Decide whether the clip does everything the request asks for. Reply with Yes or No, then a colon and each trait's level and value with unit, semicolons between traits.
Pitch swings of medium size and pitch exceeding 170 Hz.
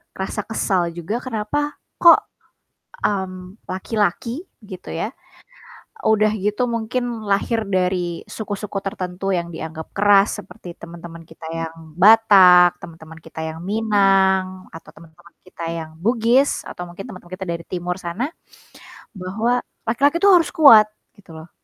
Yes: average, 4.2 semitones; high, 190 Hz